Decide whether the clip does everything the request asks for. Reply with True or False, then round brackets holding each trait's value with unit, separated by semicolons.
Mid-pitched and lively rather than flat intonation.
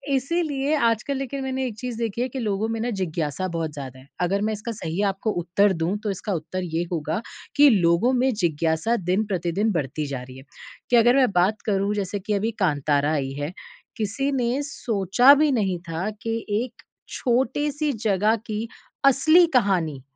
False (210 Hz; 6.3 semitones)